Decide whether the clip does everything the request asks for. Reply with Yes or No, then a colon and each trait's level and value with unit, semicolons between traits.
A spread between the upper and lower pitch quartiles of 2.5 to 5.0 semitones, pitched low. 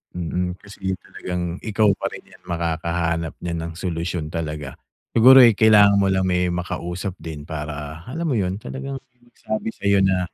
Yes: average, 3.8 semitones; very low, 90 Hz